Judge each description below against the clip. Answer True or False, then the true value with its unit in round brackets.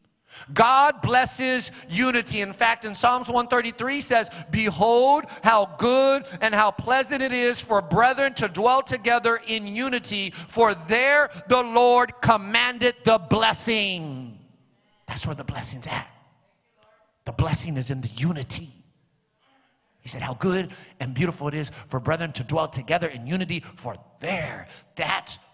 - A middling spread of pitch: False (6.5 semitones)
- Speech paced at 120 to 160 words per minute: True (140 wpm)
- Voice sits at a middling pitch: False (220 Hz)